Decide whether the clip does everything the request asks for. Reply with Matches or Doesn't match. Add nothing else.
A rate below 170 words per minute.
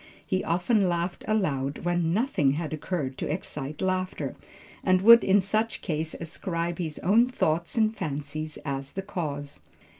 Matches